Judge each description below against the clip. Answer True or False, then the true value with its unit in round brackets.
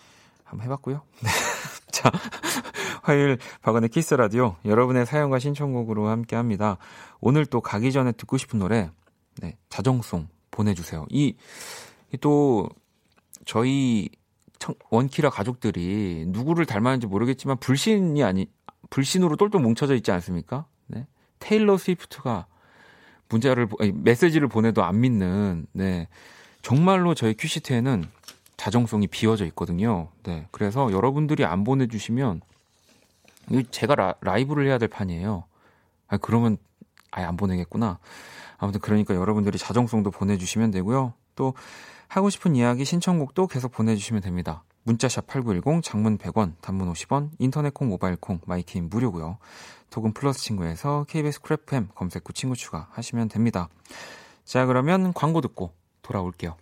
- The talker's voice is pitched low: True (115 Hz)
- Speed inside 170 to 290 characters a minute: False (315 characters per minute)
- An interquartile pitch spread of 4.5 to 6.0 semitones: True (5.4 semitones)